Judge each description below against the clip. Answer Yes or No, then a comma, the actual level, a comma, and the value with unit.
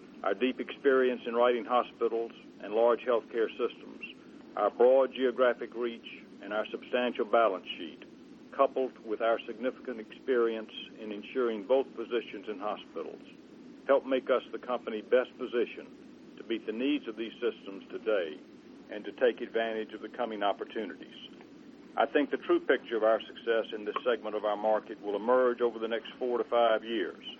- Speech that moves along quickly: No, average, 165 wpm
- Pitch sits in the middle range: No, low, 125 Hz